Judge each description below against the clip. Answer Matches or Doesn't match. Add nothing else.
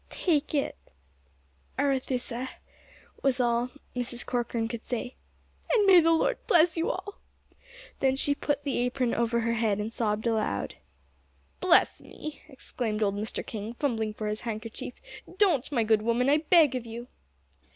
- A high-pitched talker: Matches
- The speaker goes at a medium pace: Matches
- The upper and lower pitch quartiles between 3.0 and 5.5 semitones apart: Matches